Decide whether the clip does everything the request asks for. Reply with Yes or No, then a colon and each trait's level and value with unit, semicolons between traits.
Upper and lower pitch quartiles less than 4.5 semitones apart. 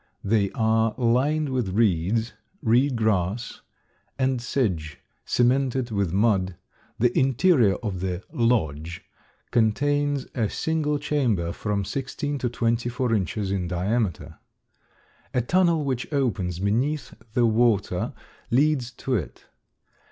No: average, 4.9 semitones